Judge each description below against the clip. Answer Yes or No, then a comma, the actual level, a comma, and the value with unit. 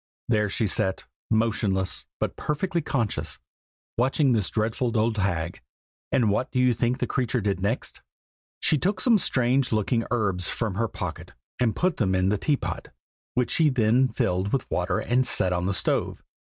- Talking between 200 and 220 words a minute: No, average, 170 wpm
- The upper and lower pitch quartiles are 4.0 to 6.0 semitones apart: Yes, average, 4.3 semitones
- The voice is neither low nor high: No, low, 115 Hz